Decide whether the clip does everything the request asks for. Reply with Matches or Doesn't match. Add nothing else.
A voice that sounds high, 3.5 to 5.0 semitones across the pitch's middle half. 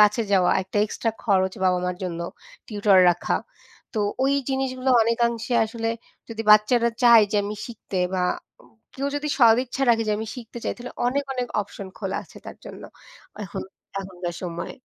Matches